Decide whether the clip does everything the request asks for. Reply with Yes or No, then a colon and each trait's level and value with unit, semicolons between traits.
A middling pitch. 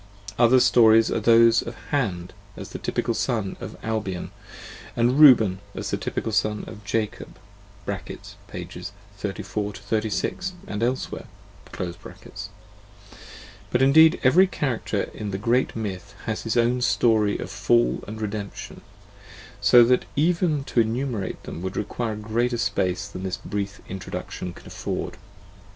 No: low, 110 Hz